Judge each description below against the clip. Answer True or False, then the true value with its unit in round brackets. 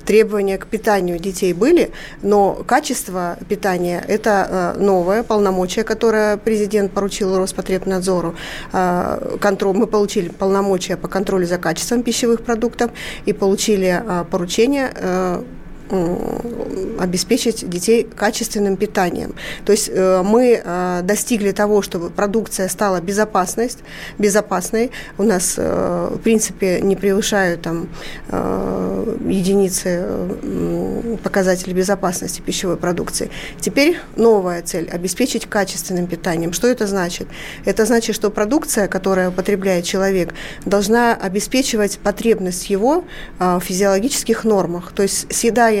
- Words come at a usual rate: False (105 wpm)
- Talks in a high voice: True (200 Hz)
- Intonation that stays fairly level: False (3.0 semitones)